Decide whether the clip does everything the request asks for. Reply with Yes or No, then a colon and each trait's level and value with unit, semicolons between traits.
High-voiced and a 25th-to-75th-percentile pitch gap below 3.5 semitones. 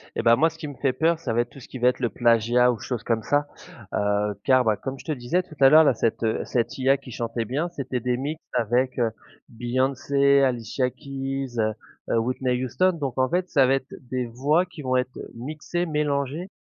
No: low, 130 Hz; average, 3.0 semitones